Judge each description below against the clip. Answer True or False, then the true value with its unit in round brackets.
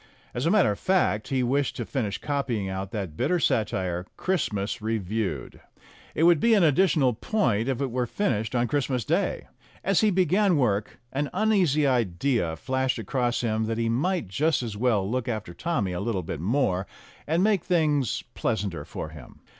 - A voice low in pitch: True (125 Hz)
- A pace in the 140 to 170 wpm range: False (180 wpm)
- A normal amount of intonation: False (6.7 semitones)